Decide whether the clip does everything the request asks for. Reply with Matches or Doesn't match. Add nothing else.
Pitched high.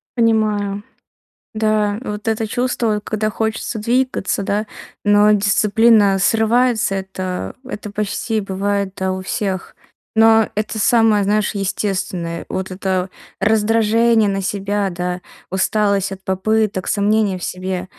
Matches